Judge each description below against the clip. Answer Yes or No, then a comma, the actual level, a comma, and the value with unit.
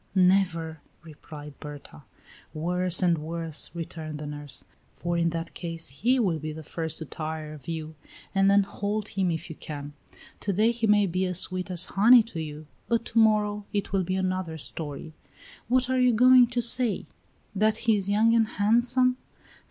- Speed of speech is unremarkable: Yes, average, 185 wpm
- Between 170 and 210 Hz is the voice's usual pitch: Yes, medium, 185 Hz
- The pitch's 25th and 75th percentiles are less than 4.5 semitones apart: No, average, 5.0 semitones